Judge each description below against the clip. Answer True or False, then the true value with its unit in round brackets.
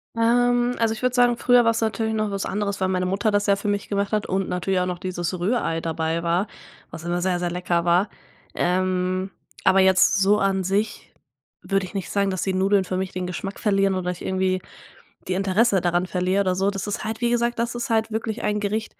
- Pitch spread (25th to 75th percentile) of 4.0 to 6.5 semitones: False (2.9 semitones)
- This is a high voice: True (195 Hz)